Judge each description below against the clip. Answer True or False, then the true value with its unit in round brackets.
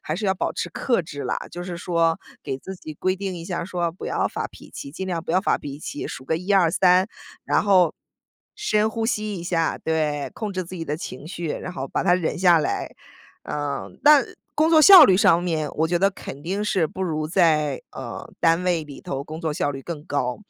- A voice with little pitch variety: False (3.5 semitones)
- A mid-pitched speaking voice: True (170 Hz)